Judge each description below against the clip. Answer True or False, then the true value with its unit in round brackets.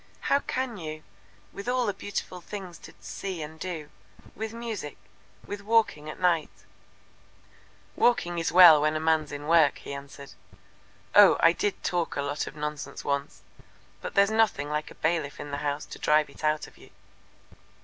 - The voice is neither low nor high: True (165 Hz)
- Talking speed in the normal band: True (180 wpm)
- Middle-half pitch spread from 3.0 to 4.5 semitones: False (5.0 semitones)